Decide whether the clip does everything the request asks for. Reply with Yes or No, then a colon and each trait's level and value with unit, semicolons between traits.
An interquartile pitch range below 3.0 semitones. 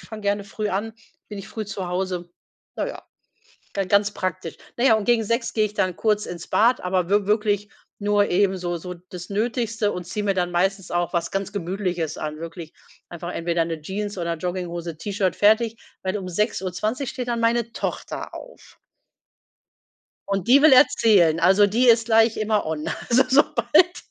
No: average, 3.7 semitones